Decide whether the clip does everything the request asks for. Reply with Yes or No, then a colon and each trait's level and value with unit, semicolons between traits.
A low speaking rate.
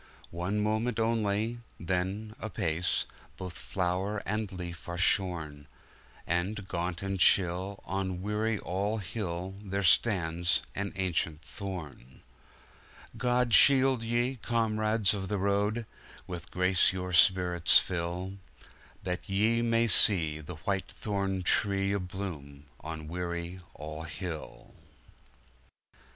Yes: slow, 110 wpm